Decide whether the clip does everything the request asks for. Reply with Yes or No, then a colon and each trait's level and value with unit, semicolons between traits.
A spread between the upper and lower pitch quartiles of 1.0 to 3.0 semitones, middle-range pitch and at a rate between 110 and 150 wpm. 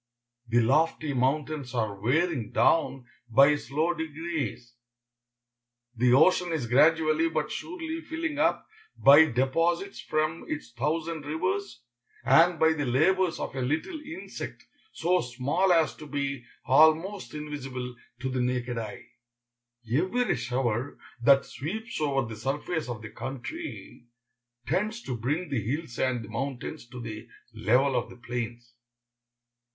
No: average, 5.0 semitones; medium, 145 Hz; slow, 135 wpm